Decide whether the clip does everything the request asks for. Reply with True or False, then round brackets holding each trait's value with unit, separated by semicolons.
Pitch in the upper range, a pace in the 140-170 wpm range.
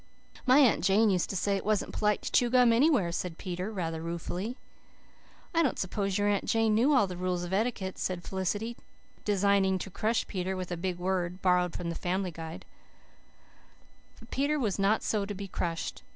False (195 Hz; 195 wpm)